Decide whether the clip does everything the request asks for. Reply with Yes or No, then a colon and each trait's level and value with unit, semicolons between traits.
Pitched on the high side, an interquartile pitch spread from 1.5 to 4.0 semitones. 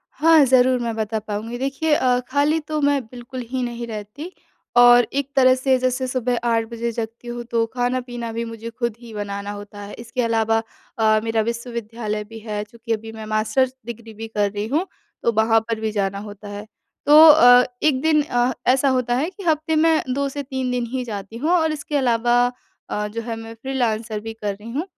Yes: high, 235 Hz; average, 2.8 semitones